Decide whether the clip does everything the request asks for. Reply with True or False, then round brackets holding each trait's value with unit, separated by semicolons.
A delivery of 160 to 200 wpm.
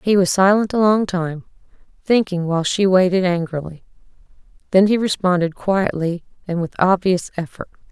False (145 wpm)